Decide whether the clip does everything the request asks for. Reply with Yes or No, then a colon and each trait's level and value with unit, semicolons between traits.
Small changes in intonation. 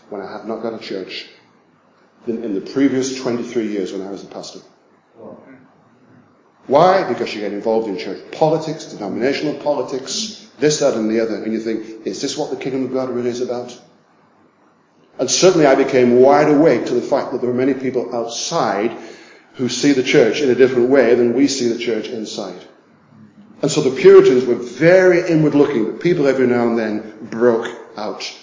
No: average, 3.8 semitones